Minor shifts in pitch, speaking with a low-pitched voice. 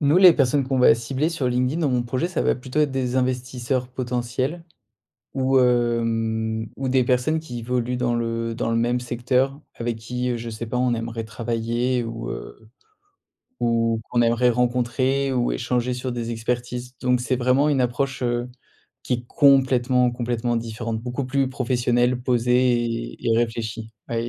Yes: narrow, 1.6 semitones; low, 125 Hz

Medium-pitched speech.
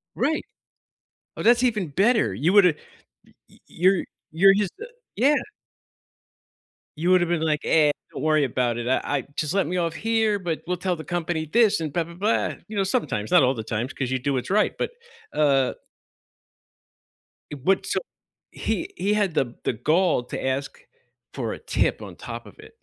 Yes: medium, 170 Hz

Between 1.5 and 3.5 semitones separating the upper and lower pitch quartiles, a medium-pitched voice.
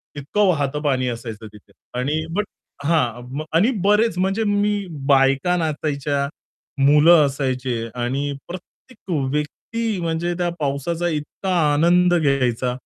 No: average, 4.7 semitones; medium, 150 Hz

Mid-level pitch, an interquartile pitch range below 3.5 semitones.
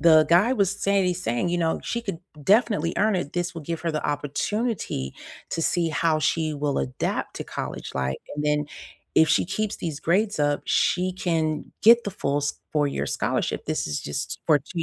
No: medium, 165 Hz; average, 4.2 semitones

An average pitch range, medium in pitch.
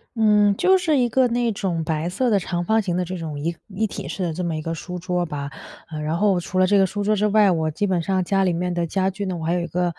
Yes: average, 3.4 semitones; medium, 180 Hz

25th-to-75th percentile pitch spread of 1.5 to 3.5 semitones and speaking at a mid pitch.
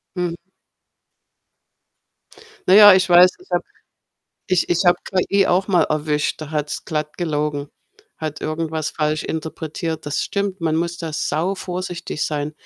Yes: average, 2.9 semitones; medium, 160 Hz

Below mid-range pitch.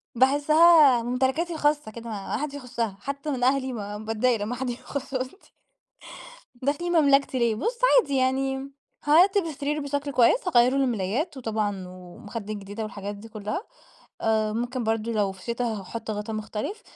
No: high, 245 Hz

